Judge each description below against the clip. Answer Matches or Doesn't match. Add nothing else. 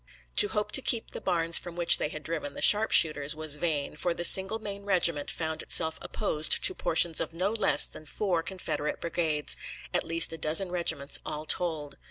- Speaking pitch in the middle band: Matches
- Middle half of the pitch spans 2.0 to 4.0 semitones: Matches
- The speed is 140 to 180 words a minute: Doesn't match